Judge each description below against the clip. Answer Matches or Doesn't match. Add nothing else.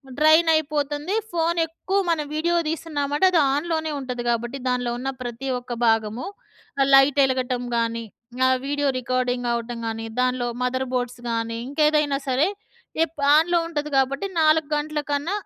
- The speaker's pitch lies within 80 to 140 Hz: Doesn't match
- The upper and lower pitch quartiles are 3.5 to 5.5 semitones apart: Matches